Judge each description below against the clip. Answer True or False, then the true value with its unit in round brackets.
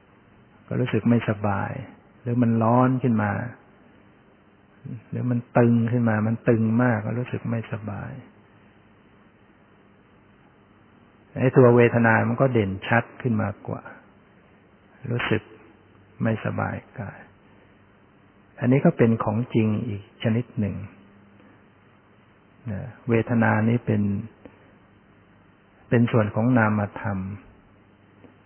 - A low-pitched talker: True (110 Hz)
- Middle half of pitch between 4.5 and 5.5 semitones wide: False (2.7 semitones)